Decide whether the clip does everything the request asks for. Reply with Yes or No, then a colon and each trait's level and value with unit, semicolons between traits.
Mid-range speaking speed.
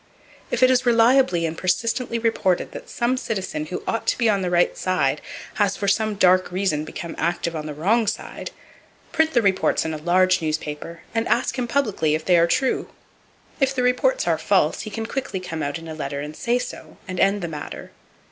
No: fast, 210 wpm